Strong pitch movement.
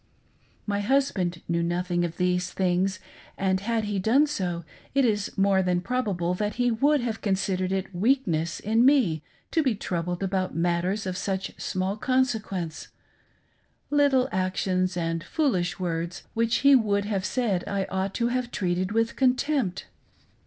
No: average, 4.5 semitones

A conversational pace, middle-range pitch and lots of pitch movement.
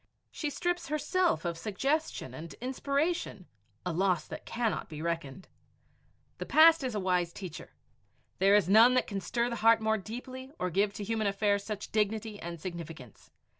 No: average, 170 wpm; high, 210 Hz; wide, 5.8 semitones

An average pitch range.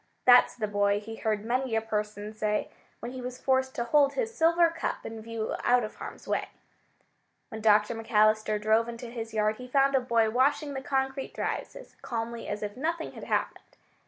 Yes: average, 3.7 semitones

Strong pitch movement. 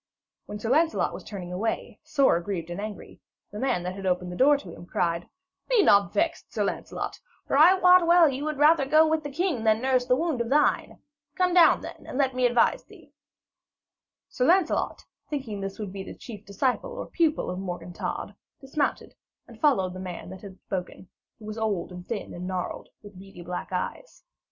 Yes: wide, 8.0 semitones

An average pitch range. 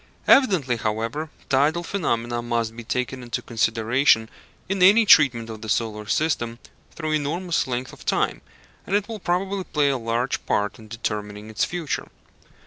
No: wide, 6.2 semitones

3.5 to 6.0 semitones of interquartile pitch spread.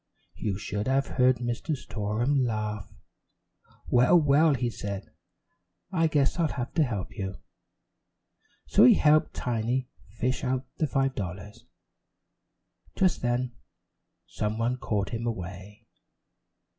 Yes: average, 4.3 semitones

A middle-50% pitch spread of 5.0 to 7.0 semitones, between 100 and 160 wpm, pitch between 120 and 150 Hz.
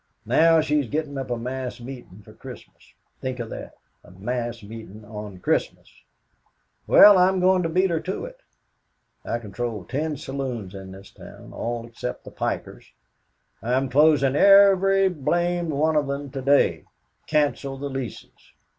Yes: wide, 5.4 semitones; average, 155 wpm; low, 135 Hz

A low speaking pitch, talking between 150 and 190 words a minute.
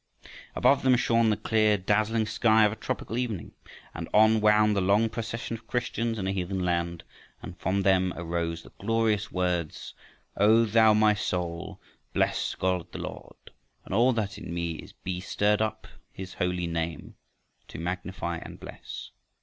Yes: low, 100 Hz; average, 165 wpm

